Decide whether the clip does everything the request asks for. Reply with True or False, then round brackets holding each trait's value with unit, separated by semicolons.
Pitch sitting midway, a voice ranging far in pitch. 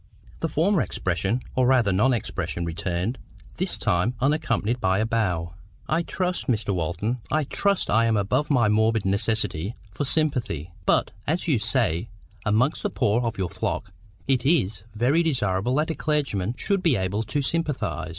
False (115 Hz; 6.5 semitones)